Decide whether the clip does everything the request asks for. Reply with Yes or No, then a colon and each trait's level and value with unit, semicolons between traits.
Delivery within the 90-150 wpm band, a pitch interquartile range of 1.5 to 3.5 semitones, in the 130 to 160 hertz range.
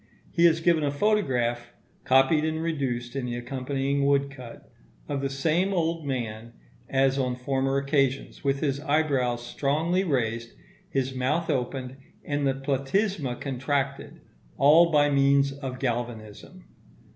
Yes: slow, 135 wpm; average, 2.7 semitones; low, 135 Hz